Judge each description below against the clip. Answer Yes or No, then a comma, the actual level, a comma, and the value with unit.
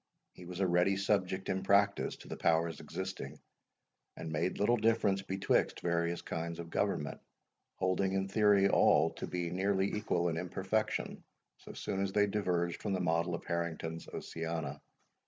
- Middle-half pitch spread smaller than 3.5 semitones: Yes, narrow, 2.6 semitones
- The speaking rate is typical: Yes, average, 160 wpm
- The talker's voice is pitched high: No, very low, 95 Hz